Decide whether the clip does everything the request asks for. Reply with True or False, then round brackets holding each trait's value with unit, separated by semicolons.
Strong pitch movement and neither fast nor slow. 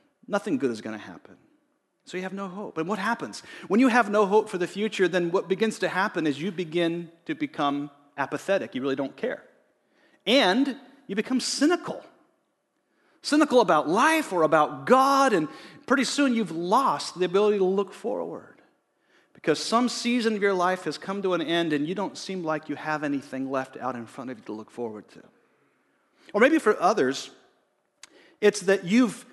True (7.1 semitones; 190 wpm)